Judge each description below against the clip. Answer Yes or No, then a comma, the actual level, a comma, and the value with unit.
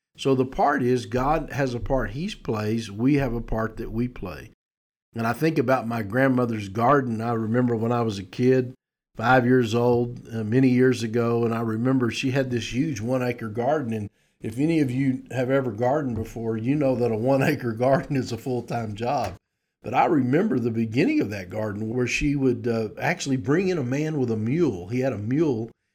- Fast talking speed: Yes, fast, 215 wpm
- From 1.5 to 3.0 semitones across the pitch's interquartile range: Yes, narrow, 2.6 semitones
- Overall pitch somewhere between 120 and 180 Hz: Yes, low, 125 Hz